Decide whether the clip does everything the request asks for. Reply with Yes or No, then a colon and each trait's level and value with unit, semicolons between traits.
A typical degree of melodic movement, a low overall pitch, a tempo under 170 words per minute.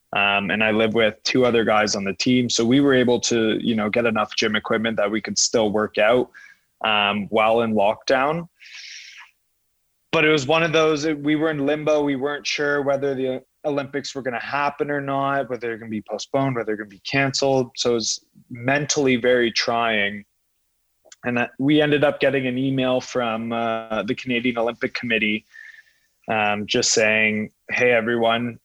No: average, 4.3 semitones; low, 125 Hz; average, 195 wpm